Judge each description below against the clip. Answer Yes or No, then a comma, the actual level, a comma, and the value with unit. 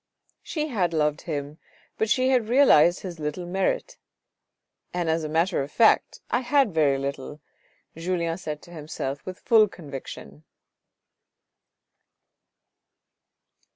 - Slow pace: Yes, slow, 130 wpm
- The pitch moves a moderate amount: No, wide, 5.8 semitones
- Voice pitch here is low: No, medium, 170 Hz